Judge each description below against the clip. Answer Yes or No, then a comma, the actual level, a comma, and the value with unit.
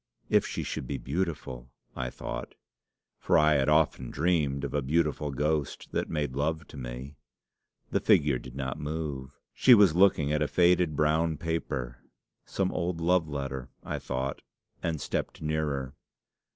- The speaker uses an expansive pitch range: No, average, 3.1 semitones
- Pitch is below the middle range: Yes, very low, 75 Hz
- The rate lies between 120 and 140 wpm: No, average, 155 wpm